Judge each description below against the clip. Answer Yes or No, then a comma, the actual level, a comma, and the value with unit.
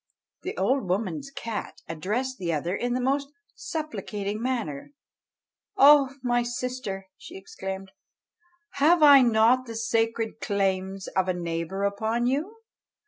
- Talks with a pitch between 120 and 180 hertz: No, high, 230 Hz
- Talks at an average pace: No, slow, 130 wpm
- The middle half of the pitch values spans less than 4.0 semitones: No, average, 5.2 semitones